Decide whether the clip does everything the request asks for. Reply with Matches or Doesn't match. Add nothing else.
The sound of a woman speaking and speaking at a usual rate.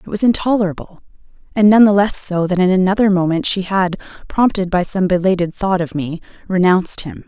Matches